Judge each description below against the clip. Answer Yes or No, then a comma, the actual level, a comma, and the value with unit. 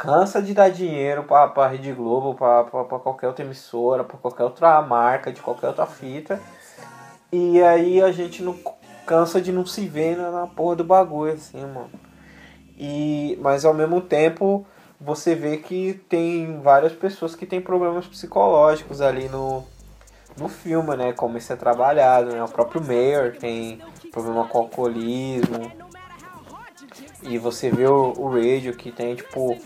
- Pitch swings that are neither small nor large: No, wide, 6.0 semitones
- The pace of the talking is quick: No, average, 160 wpm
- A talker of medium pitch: Yes, medium, 145 Hz